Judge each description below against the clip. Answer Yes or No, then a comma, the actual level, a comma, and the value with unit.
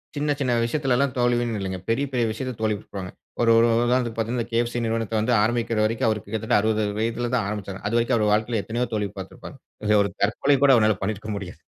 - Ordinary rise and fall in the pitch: No, narrow, 2.1 semitones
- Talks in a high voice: No, low, 115 Hz